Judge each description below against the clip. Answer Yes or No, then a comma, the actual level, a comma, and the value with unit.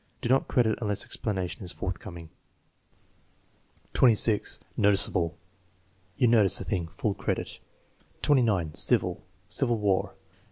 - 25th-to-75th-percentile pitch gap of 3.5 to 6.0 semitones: Yes, average, 4.0 semitones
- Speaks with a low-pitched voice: Yes, low, 105 Hz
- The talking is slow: Yes, slow, 110 wpm